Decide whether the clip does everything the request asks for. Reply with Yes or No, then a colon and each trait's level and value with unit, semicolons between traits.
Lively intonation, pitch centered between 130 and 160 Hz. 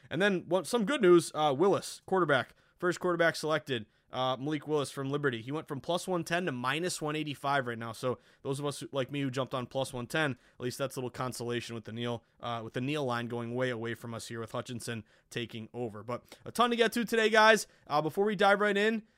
Yes: wide, 6.0 semitones; medium, 140 Hz